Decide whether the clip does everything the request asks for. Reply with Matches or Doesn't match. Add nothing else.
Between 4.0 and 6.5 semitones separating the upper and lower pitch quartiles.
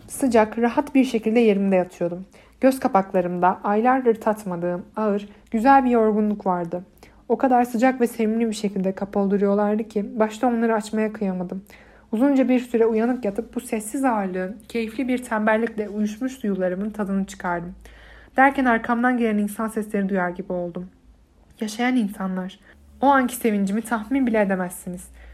Doesn't match